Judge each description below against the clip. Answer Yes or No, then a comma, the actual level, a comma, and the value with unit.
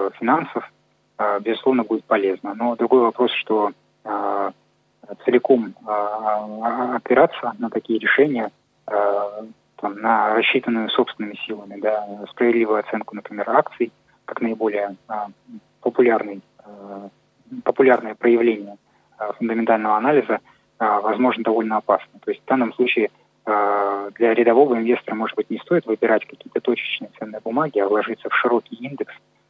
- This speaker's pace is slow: Yes, slow, 105 wpm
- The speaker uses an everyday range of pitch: No, narrow, 2.3 semitones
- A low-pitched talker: Yes, low, 110 Hz